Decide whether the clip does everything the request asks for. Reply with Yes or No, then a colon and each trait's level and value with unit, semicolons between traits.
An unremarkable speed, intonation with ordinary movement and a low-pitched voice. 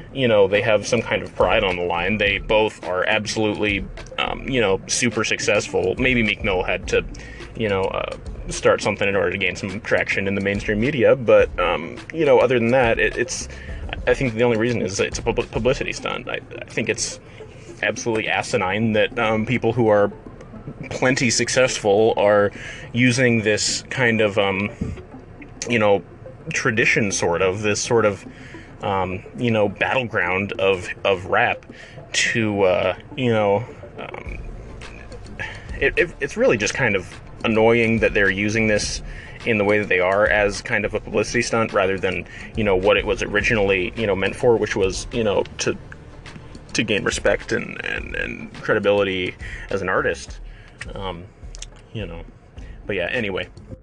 Yes: average, 175 wpm; average, 3.4 semitones; low, 110 Hz